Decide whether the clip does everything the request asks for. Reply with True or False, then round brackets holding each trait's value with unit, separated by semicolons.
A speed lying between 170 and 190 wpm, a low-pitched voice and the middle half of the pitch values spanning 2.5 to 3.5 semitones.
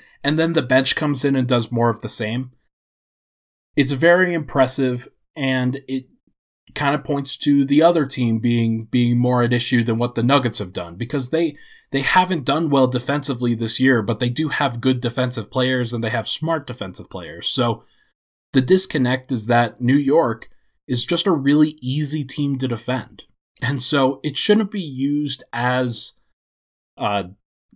True (175 wpm; 130 Hz; 3.1 semitones)